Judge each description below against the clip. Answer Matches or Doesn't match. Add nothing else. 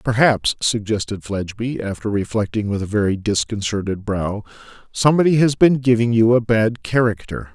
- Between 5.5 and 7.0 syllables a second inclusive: Doesn't match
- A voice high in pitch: Doesn't match